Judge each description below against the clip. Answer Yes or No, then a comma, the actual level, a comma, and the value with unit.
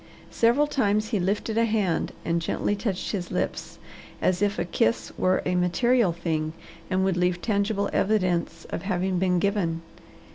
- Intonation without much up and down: No, average, 3.0 semitones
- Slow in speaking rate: No, average, 160 wpm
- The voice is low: No, high, 190 Hz